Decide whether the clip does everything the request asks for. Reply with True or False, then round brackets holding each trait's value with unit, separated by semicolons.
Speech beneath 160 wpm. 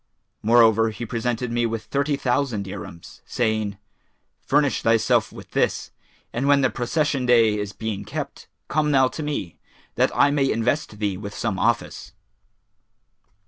True (145 wpm)